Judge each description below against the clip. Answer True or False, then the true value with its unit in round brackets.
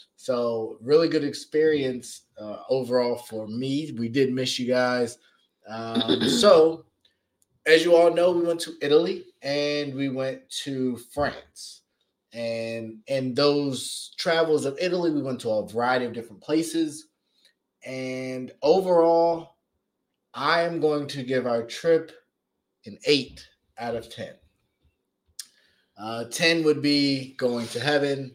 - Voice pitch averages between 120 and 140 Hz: True (135 Hz)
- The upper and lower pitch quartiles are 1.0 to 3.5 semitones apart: False (4.2 semitones)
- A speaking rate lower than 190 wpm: True (135 wpm)